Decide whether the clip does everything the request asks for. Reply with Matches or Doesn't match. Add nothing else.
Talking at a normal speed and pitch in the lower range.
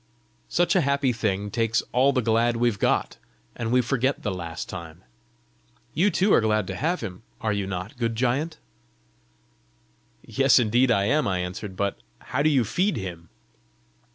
Matches